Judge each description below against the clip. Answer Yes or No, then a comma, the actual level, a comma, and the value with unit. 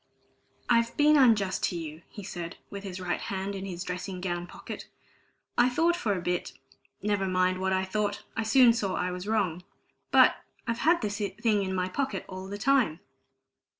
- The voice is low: No, high, 195 Hz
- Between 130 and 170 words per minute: No, average, 185 wpm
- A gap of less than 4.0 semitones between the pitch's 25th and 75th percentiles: Yes, average, 3.6 semitones